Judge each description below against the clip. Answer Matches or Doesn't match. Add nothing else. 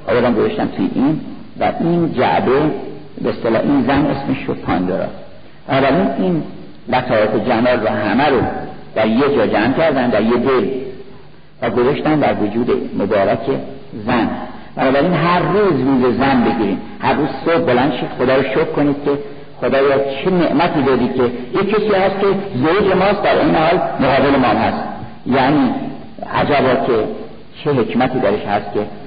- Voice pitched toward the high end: Doesn't match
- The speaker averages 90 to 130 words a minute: Doesn't match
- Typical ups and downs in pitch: Doesn't match